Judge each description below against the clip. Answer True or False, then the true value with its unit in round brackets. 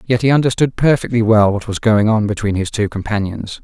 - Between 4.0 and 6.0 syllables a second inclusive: True (5.7 syllables/s)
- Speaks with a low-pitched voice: True (110 Hz)